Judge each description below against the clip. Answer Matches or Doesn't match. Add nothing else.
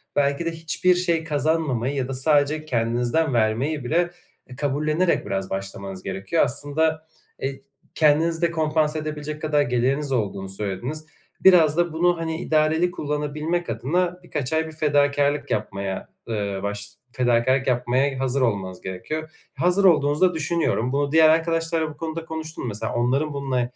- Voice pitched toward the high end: Doesn't match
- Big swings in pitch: Doesn't match